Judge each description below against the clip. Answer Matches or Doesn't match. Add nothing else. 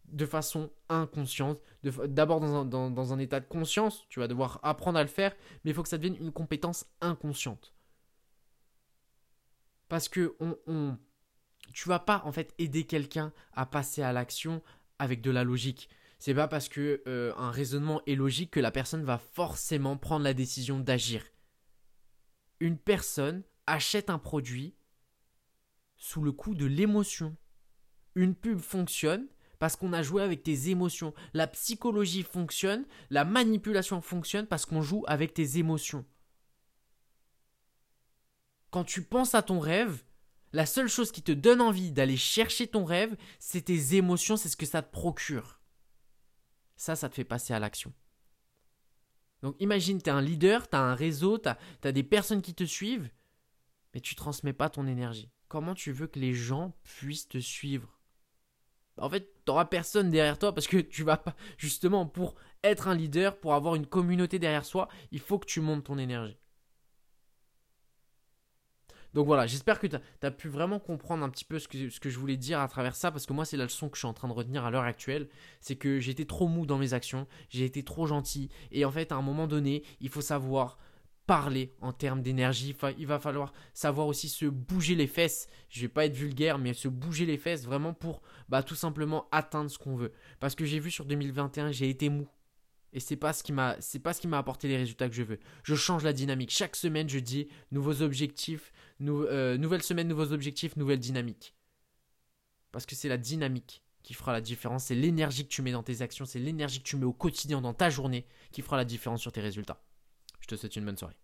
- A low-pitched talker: Doesn't match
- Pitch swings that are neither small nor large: Matches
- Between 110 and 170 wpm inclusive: Doesn't match